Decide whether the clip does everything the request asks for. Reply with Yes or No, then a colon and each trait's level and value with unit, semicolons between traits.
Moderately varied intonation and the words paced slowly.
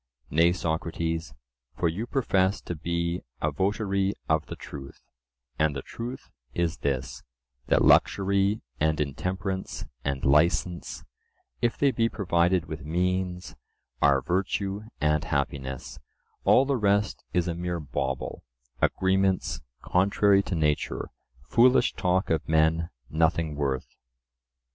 Yes: average, 4.1 semitones; slow, 115 wpm